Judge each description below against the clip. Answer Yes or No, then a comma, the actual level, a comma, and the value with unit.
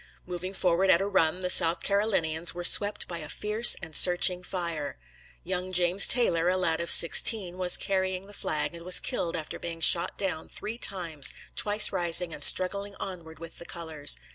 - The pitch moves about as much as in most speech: No, narrow, 2.3 semitones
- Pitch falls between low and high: Yes, medium, 180 Hz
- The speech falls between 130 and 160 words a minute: No, average, 185 wpm